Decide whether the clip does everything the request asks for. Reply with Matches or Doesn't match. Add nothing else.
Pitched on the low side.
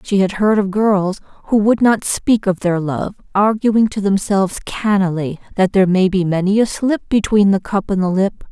Doesn't match